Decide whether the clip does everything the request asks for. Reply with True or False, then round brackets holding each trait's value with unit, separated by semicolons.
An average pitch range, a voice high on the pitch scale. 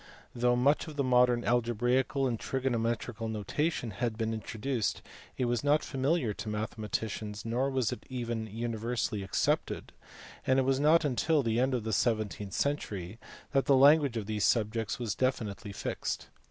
False (3.2 semitones; 120 Hz)